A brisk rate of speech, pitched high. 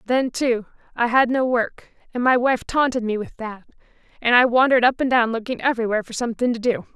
Yes: fast, 215 wpm; high, 240 Hz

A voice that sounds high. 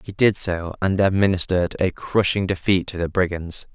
No: very low, 95 Hz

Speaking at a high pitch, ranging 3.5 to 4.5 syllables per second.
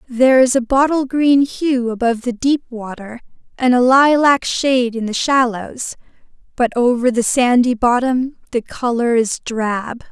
Yes: very high, 250 Hz; 4.4 syllables/s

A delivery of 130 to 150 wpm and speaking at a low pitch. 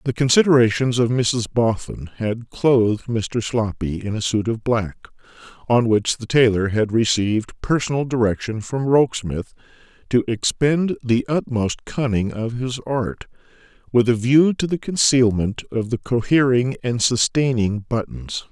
Yes: average, 145 wpm; low, 120 Hz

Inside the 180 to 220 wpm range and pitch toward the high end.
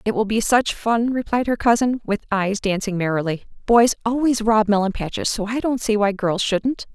Yes: fast, 205 wpm; high, 215 Hz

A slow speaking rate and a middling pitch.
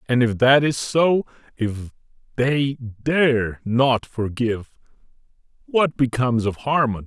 No: slow, 120 wpm; low, 125 Hz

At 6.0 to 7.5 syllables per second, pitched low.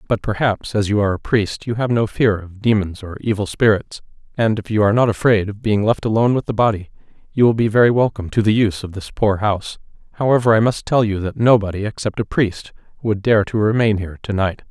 Yes: 6.2 syllables/s; low, 105 Hz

